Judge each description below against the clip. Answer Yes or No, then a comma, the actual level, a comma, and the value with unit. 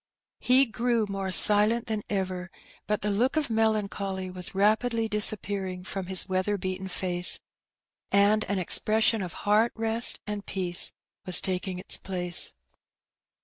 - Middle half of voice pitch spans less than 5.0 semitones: Yes, average, 2.8 semitones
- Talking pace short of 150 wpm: Yes, average, 140 wpm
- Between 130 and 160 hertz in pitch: No, high, 200 Hz